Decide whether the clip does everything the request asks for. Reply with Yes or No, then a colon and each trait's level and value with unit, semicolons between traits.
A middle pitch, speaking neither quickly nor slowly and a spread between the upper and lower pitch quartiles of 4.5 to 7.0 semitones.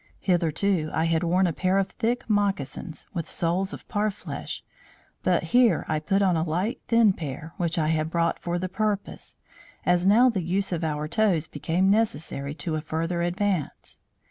No: medium, 175 Hz; average, 175 wpm; average, 3.8 semitones